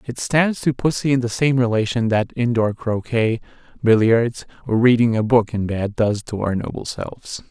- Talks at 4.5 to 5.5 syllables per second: Yes, 4.8 syllables/s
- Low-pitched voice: Yes, low, 115 Hz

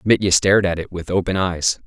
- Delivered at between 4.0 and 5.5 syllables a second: No, 5.8 syllables/s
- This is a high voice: No, very low, 90 Hz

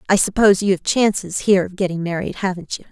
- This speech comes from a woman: Yes, female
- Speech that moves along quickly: Yes, fast, 225 wpm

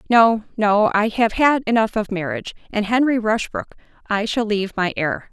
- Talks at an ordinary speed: Yes, average, 145 wpm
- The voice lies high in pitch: Yes, high, 215 Hz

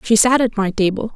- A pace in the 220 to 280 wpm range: Yes, fast, 260 wpm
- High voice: Yes, high, 215 Hz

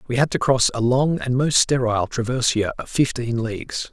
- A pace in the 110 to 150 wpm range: No, average, 200 wpm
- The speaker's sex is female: No, male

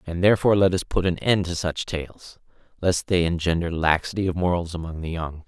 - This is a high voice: No, very low, 85 Hz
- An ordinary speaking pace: No, fast, 210 wpm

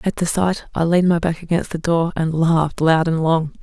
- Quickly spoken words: Yes, fast, 250 wpm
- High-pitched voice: No, medium, 165 Hz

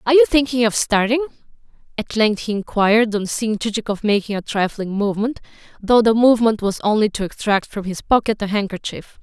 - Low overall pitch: No, high, 220 Hz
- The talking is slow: No, average, 180 wpm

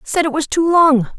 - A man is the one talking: No, female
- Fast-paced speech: Yes, fast, 255 wpm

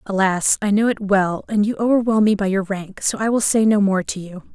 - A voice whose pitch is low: No, high, 205 Hz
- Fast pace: Yes, fast, 265 wpm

